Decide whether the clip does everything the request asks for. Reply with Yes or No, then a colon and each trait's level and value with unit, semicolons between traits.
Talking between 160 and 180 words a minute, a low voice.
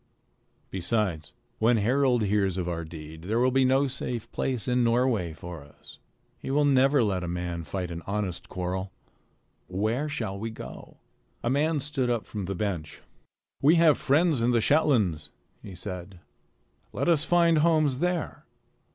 Yes: average, 170 wpm; low, 115 Hz